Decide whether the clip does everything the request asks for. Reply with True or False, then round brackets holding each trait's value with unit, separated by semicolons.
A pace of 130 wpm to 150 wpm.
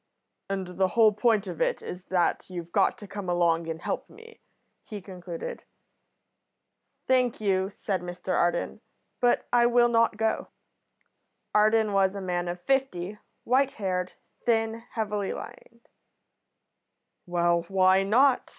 True (135 wpm)